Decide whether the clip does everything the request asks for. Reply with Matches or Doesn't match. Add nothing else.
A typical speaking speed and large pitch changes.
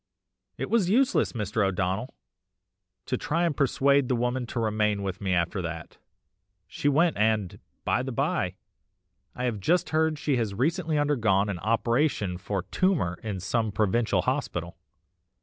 Matches